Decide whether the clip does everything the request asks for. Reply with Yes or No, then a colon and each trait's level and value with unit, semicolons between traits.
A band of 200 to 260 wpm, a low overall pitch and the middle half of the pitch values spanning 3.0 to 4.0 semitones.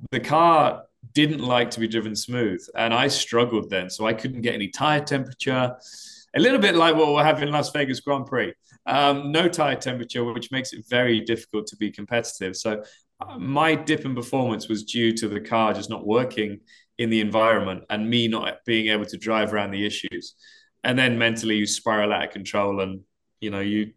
Yes: fast, 205 wpm; low, 115 Hz; average, 3.7 semitones